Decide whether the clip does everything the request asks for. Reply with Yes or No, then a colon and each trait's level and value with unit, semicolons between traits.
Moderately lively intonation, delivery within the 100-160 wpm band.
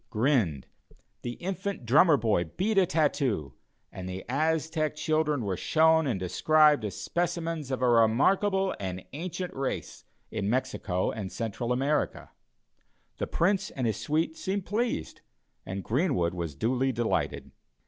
No: wide, 6.8 semitones; average, 140 wpm